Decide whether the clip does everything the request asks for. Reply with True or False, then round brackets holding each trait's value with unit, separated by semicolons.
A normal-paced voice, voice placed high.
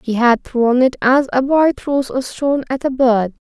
False (225 wpm; 255 Hz)